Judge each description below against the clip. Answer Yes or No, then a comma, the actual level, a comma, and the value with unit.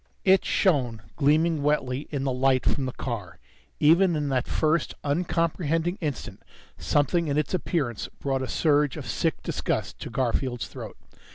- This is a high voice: No, medium, 145 Hz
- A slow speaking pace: No, average, 155 wpm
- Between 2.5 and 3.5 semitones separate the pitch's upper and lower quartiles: No, average, 3.9 semitones